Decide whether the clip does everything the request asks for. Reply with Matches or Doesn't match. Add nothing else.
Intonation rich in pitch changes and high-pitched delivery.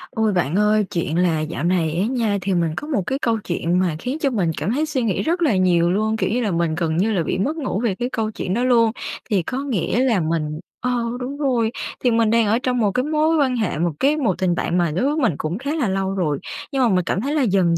Matches